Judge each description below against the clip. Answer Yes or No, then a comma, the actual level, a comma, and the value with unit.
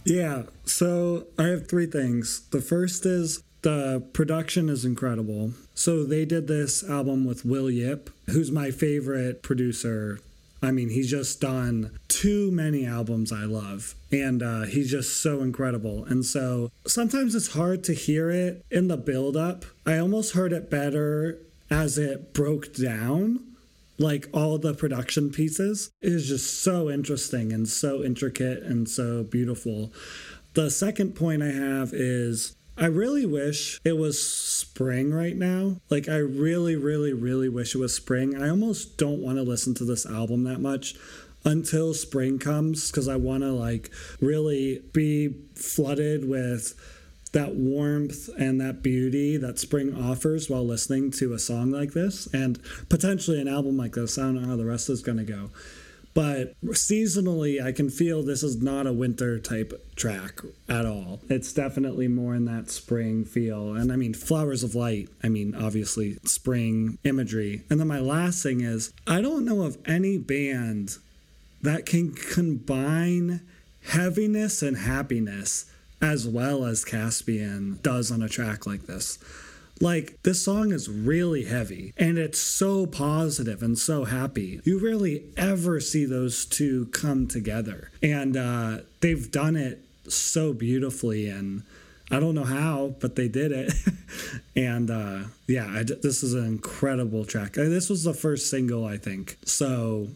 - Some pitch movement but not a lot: Yes, average, 4.8 semitones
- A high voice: No, low, 135 Hz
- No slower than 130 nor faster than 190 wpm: Yes, average, 160 wpm